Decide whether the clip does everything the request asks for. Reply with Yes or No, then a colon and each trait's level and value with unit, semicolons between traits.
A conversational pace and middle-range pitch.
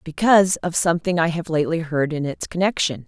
Yes: average, 195 wpm; medium, 165 Hz